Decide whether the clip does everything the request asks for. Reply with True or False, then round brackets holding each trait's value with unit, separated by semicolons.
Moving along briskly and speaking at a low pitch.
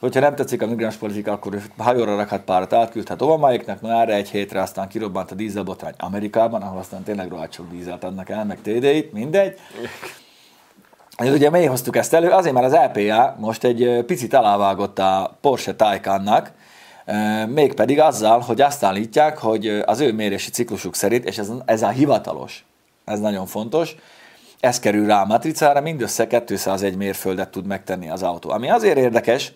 True (170 wpm; 110 Hz)